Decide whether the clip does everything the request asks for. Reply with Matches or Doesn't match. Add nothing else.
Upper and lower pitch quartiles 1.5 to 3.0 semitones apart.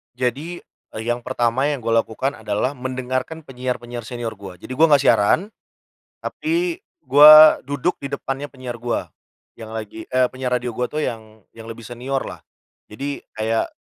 Doesn't match